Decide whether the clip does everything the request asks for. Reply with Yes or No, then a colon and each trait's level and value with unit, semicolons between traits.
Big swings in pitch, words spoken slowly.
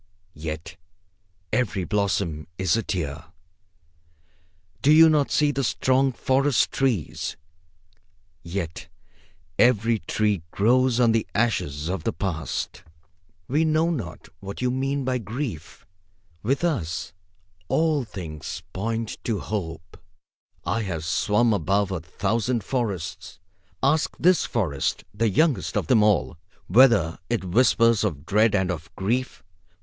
Yes: wide, 6.4 semitones; slow, 125 wpm